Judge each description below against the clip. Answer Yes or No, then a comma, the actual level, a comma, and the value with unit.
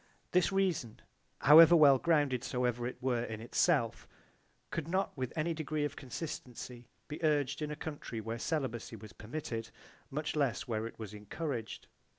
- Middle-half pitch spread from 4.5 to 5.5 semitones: Yes, average, 4.9 semitones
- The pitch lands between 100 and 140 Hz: Yes, low, 135 Hz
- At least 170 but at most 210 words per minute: No, average, 160 wpm